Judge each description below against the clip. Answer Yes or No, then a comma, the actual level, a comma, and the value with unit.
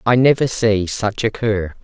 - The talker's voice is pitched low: Yes, low, 110 Hz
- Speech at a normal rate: Yes, average, 195 wpm